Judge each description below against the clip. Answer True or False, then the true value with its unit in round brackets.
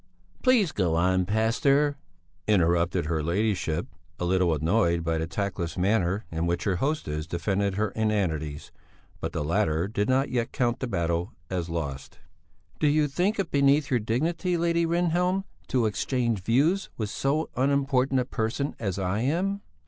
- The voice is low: True (110 Hz)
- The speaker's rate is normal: True (155 wpm)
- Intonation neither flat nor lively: False (8.2 semitones)